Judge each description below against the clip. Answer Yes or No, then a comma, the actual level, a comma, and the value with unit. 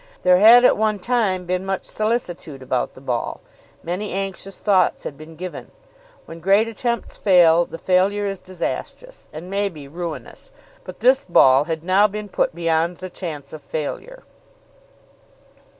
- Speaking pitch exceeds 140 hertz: Yes, medium, 185 Hz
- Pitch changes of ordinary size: Yes, average, 4.0 semitones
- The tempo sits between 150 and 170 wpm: Yes, average, 155 wpm